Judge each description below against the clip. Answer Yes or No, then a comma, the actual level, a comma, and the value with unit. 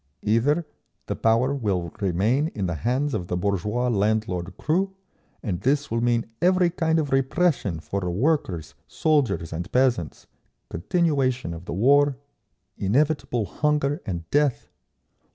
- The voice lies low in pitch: Yes, low, 120 Hz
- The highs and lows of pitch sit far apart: Yes, wide, 7.4 semitones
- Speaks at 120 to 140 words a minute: Yes, slow, 135 wpm